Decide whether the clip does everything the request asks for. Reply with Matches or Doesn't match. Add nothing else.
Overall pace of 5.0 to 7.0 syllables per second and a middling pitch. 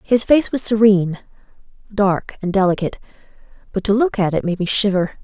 Doesn't match